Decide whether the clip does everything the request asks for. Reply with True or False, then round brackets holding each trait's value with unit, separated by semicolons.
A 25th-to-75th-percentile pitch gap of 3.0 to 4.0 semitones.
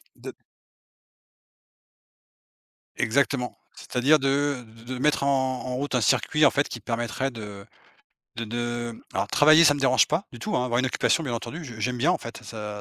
True (3.4 semitones)